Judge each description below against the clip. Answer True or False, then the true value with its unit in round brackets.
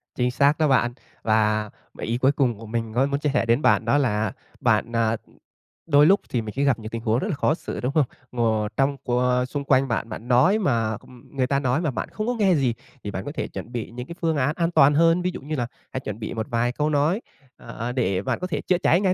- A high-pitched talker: False (130 Hz)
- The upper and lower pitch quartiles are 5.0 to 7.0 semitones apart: False (4.2 semitones)